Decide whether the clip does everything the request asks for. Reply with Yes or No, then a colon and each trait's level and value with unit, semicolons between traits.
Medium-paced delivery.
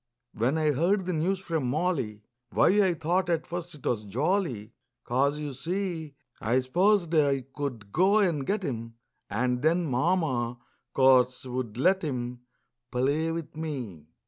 Yes: average, 150 wpm